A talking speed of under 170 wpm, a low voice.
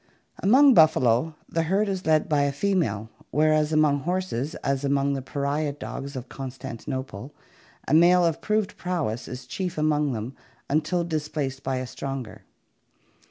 No: average, 150 wpm; medium, 150 Hz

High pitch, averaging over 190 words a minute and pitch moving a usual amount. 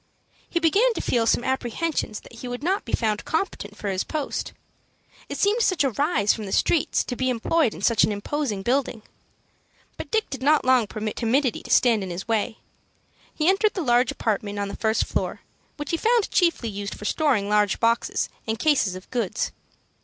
No: high, 245 Hz; average, 200 wpm; wide, 6.4 semitones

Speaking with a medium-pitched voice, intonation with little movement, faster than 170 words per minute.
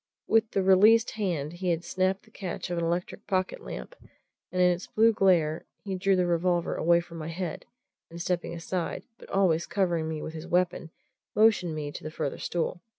Yes: medium, 175 Hz; narrow, 2.2 semitones; average, 200 wpm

